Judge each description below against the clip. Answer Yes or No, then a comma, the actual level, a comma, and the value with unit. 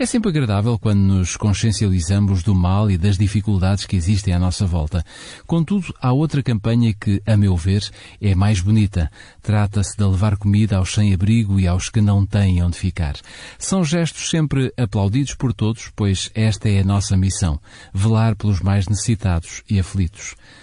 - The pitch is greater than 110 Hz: No, low, 100 Hz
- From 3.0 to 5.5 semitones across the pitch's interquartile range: No, narrow, 2.5 semitones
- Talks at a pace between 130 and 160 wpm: No, average, 170 wpm